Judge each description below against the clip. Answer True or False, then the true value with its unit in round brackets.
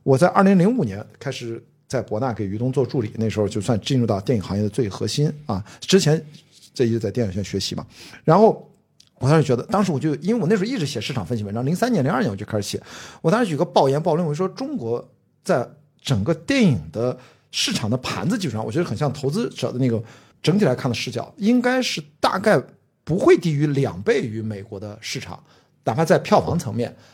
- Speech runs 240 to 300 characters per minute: False (340 characters per minute)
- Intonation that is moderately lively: False (6.3 semitones)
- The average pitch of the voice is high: False (135 Hz)